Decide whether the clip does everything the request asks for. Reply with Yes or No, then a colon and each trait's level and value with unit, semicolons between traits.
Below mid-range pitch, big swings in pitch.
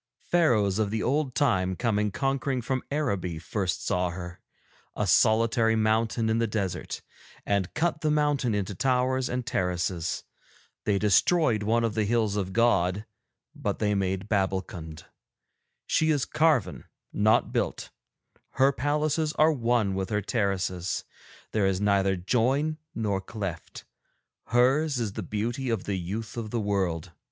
No: low, 110 Hz; average, 4.7 semitones